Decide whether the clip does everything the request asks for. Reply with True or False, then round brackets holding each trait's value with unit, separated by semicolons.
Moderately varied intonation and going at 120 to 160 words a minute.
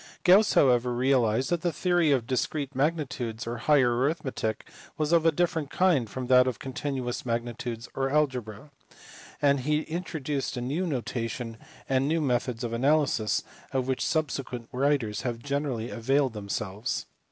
True (3.7 semitones; 150 wpm)